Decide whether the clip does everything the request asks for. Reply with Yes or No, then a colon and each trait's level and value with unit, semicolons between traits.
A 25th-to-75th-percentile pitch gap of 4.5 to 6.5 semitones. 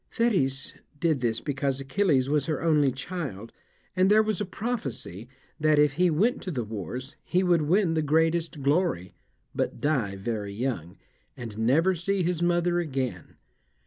Yes: wide, 5.6 semitones